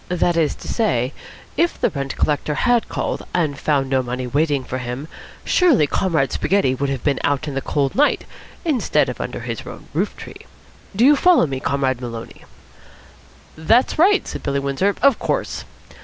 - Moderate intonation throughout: No, wide, 7.0 semitones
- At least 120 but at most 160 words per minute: No, average, 180 wpm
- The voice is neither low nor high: Yes, medium, 145 Hz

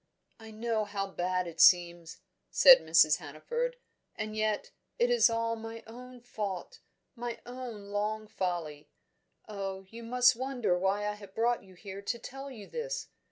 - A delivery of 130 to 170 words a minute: Yes, average, 160 wpm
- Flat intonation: No, average, 4.0 semitones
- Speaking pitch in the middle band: No, high, 215 Hz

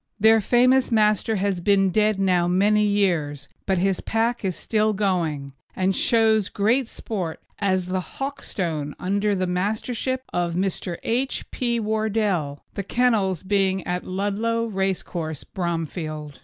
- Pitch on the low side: No, high, 195 Hz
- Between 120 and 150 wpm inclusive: Yes, average, 140 wpm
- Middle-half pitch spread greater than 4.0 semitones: No, average, 3.4 semitones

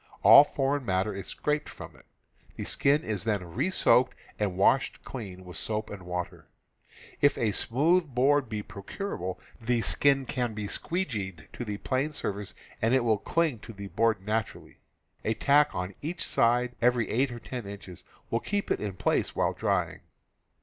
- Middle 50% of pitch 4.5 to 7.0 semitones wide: Yes, wide, 5.4 semitones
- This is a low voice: Yes, low, 115 Hz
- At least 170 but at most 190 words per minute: Yes, average, 185 wpm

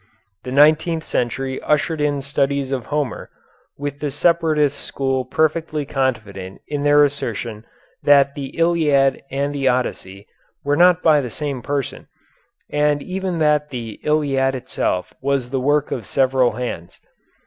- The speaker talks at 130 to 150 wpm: Yes, average, 140 wpm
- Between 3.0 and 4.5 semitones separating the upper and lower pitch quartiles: No, narrow, 2.5 semitones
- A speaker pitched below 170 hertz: Yes, medium, 140 Hz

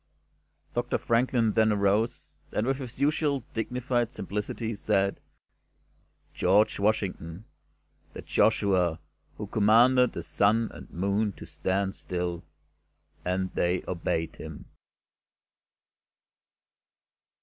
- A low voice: Yes, low, 105 Hz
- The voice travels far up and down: No, average, 3.7 semitones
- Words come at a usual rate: No, slow, 95 wpm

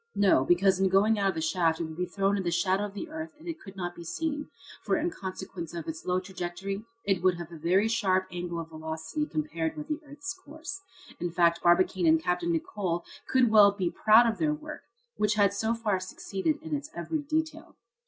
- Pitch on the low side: No, high, 190 Hz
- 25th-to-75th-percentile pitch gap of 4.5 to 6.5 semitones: Yes, average, 5.0 semitones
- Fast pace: Yes, fast, 220 wpm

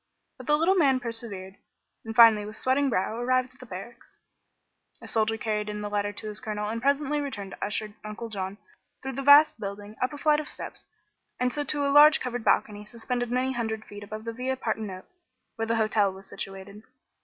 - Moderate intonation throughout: Yes, average, 3.7 semitones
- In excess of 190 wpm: Yes, fast, 205 wpm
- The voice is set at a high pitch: Yes, high, 225 Hz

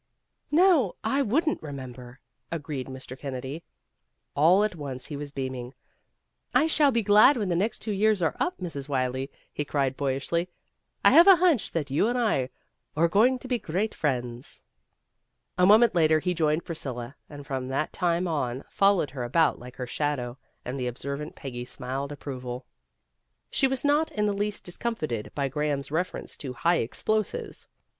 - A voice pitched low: No, medium, 155 Hz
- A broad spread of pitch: Yes, wide, 7.7 semitones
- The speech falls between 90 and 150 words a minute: No, average, 170 wpm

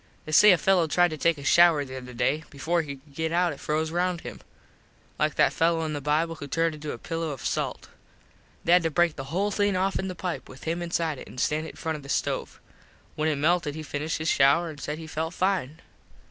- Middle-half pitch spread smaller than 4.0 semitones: Yes, average, 2.7 semitones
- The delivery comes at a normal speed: No, fast, 250 wpm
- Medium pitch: Yes, medium, 160 Hz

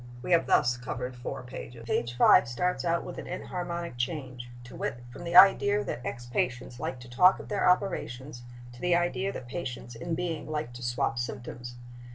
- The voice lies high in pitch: No, low, 125 Hz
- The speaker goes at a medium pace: Yes, average, 195 wpm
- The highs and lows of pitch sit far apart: Yes, wide, 6.1 semitones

